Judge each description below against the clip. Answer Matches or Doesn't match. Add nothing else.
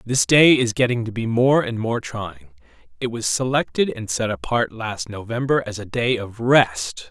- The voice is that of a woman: Doesn't match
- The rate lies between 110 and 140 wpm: Doesn't match